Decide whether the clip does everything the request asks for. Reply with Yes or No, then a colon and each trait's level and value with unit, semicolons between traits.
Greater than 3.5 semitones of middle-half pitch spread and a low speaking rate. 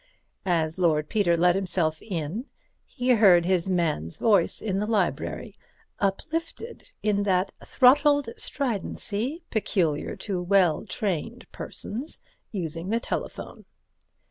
Yes: average, 4.8 semitones; slow, 115 wpm